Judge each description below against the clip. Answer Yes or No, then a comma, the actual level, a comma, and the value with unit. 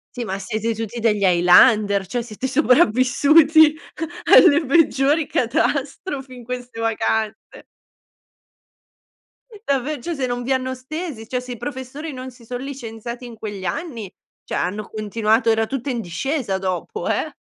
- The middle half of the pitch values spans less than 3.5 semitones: No, average, 3.8 semitones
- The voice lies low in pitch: No, high, 245 Hz